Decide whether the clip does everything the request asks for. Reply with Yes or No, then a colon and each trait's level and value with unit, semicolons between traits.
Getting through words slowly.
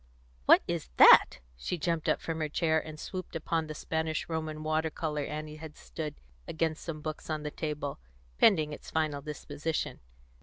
No: average, 165 wpm